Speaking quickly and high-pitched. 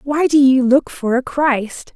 Yes: fast, 215 wpm; very high, 265 Hz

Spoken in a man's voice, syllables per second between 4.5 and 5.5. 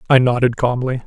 No: male; 6.0 syllables/s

